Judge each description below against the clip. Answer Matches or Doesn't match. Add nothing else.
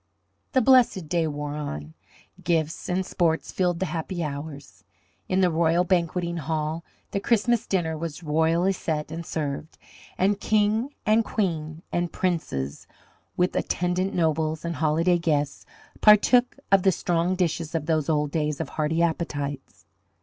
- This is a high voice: Doesn't match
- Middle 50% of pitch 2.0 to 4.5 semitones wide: Matches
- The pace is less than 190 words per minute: Matches